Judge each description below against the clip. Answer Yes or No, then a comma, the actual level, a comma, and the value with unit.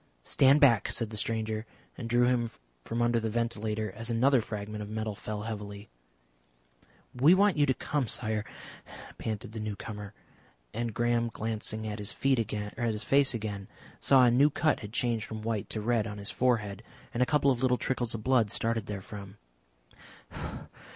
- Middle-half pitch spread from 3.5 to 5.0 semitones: No, narrow, 2.4 semitones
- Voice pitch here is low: Yes, low, 115 Hz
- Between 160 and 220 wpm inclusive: Yes, average, 165 wpm